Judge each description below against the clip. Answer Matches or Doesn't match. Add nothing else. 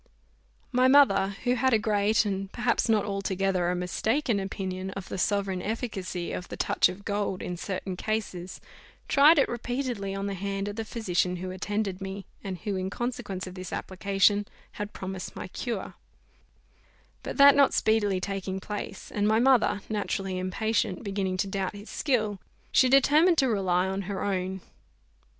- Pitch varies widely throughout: Doesn't match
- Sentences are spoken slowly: Doesn't match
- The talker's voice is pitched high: Matches